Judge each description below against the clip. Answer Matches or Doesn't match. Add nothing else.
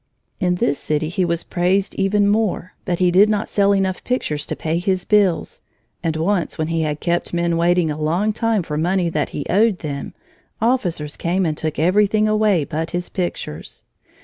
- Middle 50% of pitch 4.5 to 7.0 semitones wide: Doesn't match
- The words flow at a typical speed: Matches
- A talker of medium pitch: Matches